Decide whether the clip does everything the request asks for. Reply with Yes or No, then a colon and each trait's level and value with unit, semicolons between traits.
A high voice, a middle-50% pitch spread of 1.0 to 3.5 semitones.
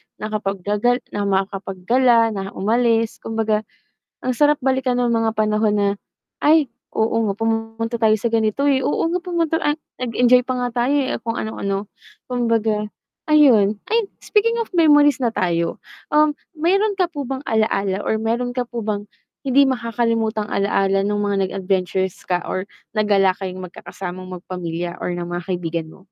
No: high, 225 Hz; average, 4.2 semitones